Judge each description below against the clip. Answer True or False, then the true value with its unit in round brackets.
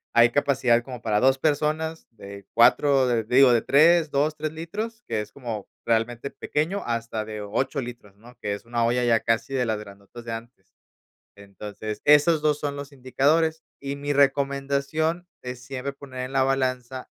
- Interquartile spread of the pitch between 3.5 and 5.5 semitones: True (3.8 semitones)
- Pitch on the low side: True (130 Hz)